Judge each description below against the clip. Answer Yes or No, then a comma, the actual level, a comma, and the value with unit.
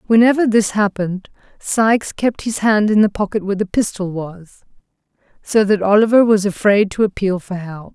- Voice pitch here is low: No, high, 205 Hz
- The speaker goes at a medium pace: Yes, average, 175 wpm